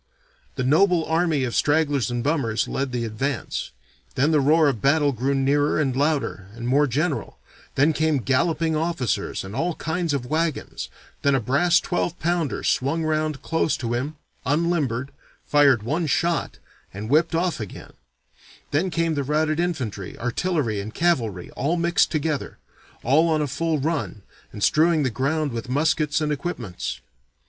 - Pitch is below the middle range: No, medium, 145 Hz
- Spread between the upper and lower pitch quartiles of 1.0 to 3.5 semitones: No, average, 4.0 semitones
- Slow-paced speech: No, average, 160 wpm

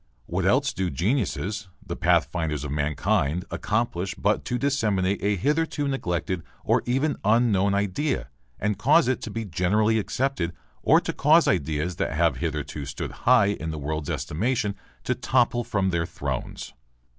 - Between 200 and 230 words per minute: No, average, 155 wpm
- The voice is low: Yes, low, 100 Hz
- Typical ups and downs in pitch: No, wide, 6.3 semitones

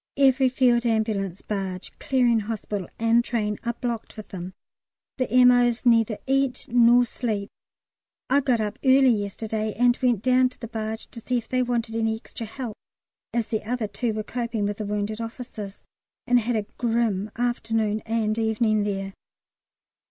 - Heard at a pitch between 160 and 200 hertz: No, high, 230 Hz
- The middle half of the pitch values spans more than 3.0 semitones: No, narrow, 2.4 semitones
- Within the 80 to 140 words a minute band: No, average, 165 wpm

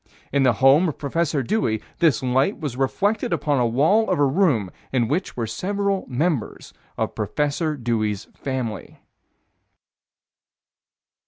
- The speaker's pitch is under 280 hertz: Yes, medium, 140 Hz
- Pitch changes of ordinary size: No, wide, 5.7 semitones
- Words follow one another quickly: No, slow, 135 wpm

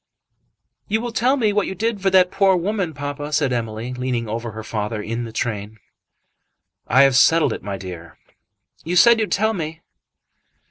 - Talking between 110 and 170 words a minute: No, average, 180 wpm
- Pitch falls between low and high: Yes, medium, 145 Hz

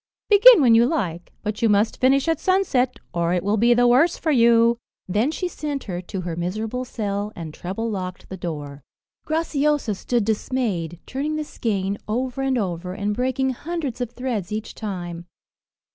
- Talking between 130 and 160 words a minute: No, average, 175 wpm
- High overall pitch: Yes, high, 230 Hz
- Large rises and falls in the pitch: Yes, wide, 5.8 semitones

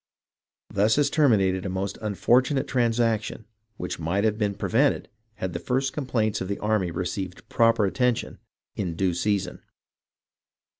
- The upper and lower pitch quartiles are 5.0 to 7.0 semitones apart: No, average, 3.8 semitones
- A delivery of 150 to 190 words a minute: No, average, 140 wpm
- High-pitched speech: No, low, 105 Hz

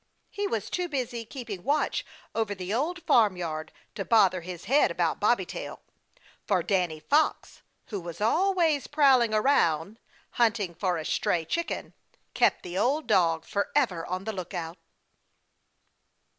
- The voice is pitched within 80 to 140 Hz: No, high, 210 Hz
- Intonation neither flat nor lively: No, wide, 7.4 semitones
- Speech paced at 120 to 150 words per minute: Yes, average, 140 wpm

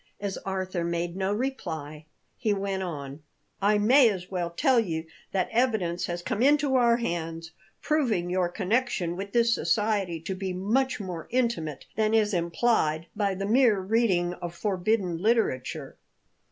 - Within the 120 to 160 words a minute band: Yes, average, 155 wpm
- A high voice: Yes, high, 195 Hz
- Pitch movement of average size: Yes, average, 4.7 semitones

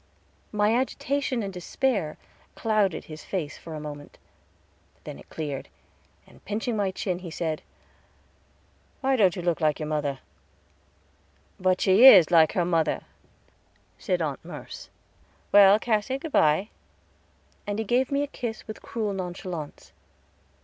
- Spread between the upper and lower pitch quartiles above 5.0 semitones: Yes, wide, 5.5 semitones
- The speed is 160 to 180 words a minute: No, average, 140 wpm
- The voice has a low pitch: No, high, 190 Hz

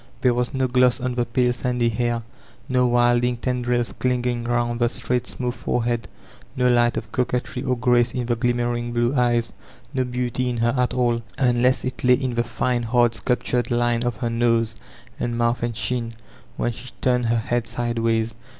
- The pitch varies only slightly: Yes, narrow, 0.9 semitones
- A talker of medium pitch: No, low, 120 Hz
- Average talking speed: Yes, average, 185 wpm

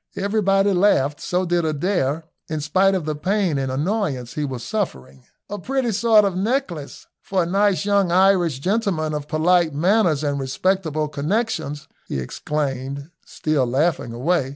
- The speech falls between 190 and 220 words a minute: No, average, 155 wpm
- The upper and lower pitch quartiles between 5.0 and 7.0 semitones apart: Yes, wide, 5.4 semitones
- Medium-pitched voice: Yes, medium, 170 Hz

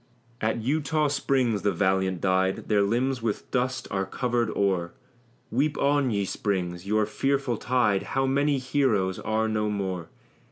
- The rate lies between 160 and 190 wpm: No, average, 150 wpm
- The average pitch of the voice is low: Yes, low, 110 Hz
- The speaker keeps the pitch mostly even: No, average, 5.1 semitones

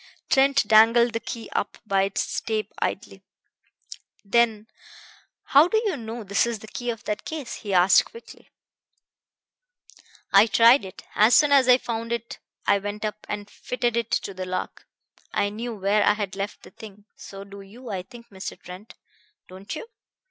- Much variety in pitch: No, average, 3.0 semitones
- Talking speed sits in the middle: Yes, average, 170 wpm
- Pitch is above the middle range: Yes, high, 220 Hz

